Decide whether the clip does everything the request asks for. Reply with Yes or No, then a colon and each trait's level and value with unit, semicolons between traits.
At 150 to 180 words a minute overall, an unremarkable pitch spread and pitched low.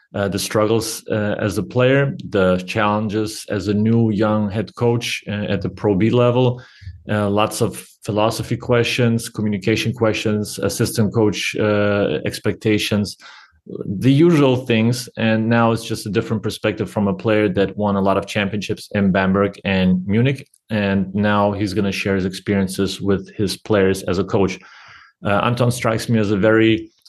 No: average, 170 wpm; narrow, 2.1 semitones; low, 105 Hz